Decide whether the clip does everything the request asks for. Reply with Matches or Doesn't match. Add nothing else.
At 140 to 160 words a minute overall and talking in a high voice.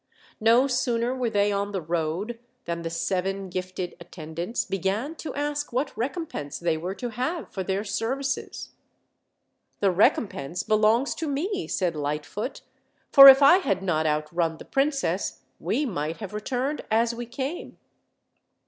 Matches